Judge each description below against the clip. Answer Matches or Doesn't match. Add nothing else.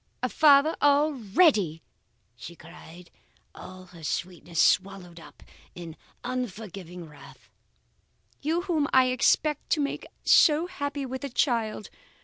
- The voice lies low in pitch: Doesn't match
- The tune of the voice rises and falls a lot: Matches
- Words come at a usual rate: Doesn't match